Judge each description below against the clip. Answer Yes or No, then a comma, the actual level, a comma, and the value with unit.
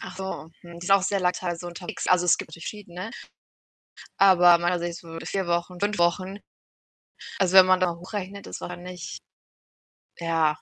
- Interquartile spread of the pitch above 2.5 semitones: No, narrow, 1.8 semitones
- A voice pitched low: No, medium, 180 Hz